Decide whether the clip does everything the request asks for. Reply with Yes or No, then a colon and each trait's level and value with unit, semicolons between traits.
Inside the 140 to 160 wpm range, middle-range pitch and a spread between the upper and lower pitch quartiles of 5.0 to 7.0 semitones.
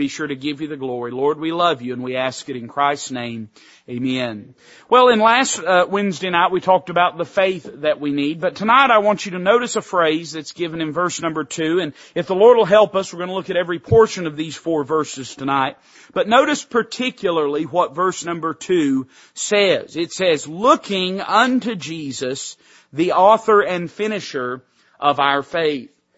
No: average, 200 wpm; medium, 170 Hz; wide, 5.6 semitones